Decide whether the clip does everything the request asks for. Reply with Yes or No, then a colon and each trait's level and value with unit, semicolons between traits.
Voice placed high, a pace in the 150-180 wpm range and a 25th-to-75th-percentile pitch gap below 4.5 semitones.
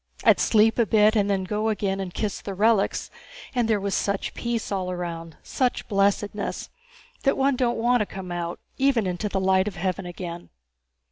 No: high, 200 Hz; average, 190 wpm; average, 3.0 semitones